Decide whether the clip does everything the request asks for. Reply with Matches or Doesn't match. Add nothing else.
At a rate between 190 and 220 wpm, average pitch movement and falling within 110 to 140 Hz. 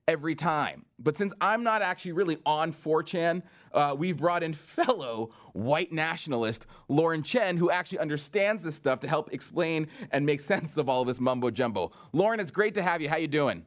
Doesn't match